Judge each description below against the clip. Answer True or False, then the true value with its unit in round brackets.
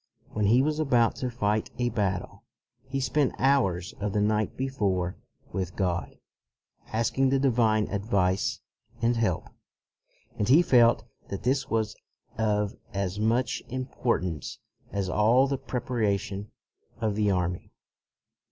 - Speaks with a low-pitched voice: True (110 Hz)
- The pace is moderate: False (130 wpm)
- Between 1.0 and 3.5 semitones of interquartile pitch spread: False (4.0 semitones)